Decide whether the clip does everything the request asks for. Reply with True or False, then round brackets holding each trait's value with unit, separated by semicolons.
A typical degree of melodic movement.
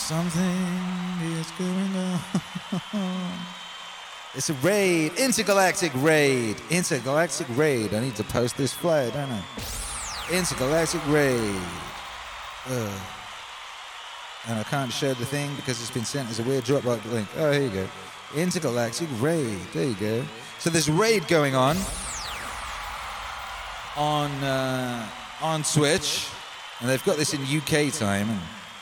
False (5.8 semitones)